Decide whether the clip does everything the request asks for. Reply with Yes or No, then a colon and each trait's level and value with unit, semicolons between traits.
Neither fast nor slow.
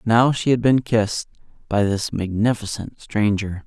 Yes: average, 145 wpm